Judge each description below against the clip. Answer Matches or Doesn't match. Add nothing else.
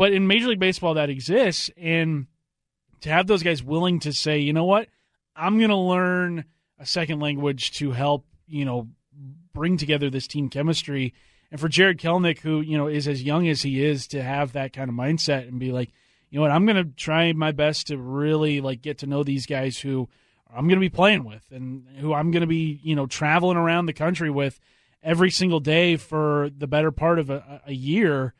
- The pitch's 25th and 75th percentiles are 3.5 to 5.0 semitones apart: Doesn't match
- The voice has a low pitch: Doesn't match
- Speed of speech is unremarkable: Doesn't match